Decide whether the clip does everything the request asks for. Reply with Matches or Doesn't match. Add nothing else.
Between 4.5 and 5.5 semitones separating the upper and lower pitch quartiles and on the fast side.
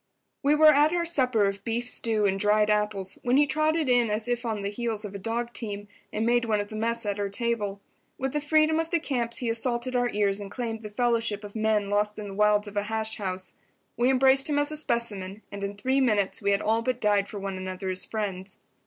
Doesn't match